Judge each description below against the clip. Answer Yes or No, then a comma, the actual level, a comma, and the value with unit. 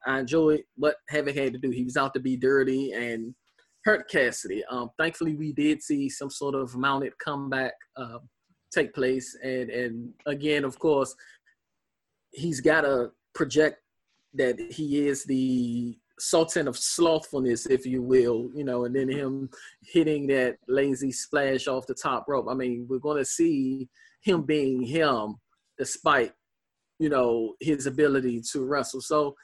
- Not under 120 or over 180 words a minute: Yes, average, 160 wpm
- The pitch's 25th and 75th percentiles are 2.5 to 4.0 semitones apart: Yes, average, 3.0 semitones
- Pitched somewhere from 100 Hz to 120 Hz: No, low, 135 Hz